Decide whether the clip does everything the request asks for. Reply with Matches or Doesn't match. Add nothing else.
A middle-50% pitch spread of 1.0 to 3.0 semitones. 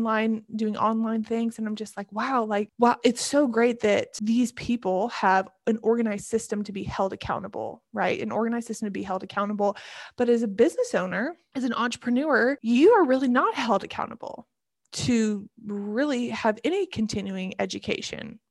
Matches